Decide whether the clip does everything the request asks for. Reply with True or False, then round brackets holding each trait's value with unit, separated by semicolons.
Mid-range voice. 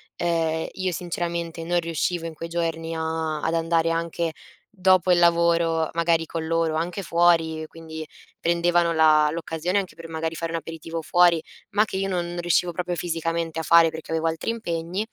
True (165 Hz)